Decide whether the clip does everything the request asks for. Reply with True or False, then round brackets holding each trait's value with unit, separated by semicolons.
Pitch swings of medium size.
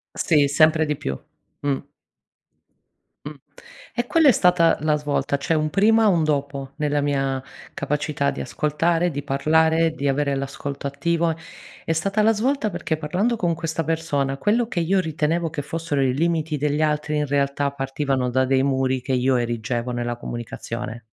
True (3.2 semitones)